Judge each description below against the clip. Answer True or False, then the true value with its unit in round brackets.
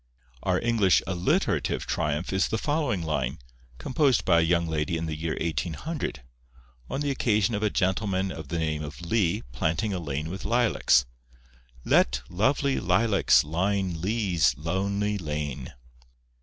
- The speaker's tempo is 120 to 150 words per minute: True (145 wpm)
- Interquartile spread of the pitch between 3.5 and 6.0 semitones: True (5.0 semitones)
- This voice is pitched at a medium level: False (90 Hz)